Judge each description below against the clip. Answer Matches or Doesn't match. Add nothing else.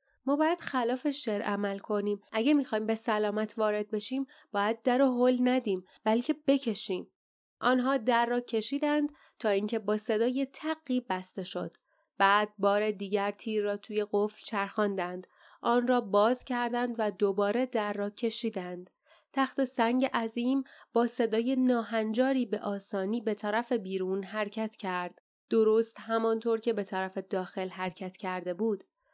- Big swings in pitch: Doesn't match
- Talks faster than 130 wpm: Matches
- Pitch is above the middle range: Matches